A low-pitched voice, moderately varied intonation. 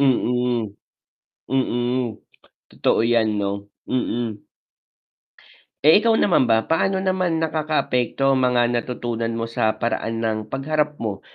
Yes: low, 120 Hz; average, 4.6 semitones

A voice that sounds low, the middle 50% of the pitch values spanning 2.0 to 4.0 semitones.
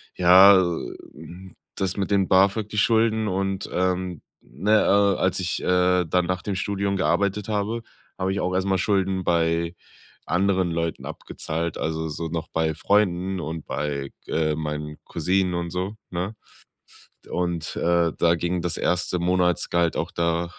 Yes: very low, 90 Hz; narrow, 2.5 semitones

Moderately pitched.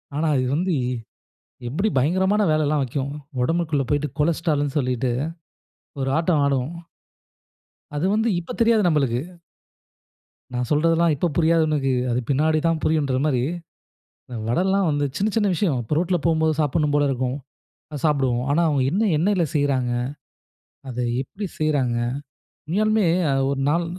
Yes: medium, 150 Hz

